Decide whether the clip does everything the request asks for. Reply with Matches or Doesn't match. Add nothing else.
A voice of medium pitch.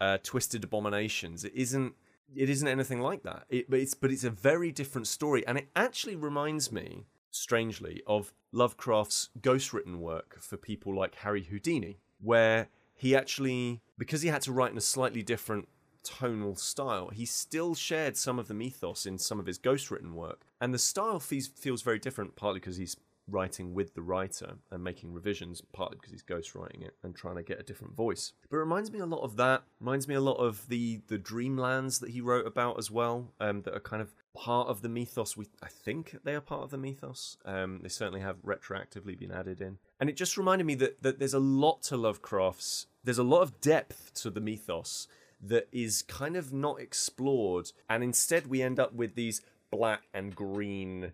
Doesn't match